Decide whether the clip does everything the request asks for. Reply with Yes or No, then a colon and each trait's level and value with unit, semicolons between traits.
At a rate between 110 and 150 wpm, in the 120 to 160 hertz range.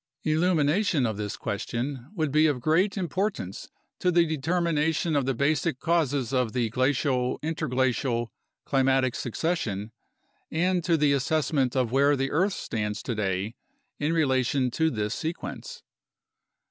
Yes: slow, 135 wpm; medium, 140 Hz